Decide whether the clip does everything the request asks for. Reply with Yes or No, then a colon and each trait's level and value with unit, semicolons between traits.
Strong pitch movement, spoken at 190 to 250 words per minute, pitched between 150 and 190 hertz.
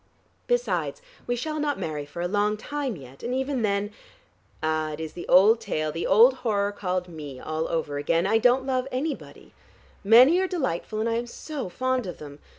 No: wide, 7.8 semitones; average, 195 wpm; high, 210 Hz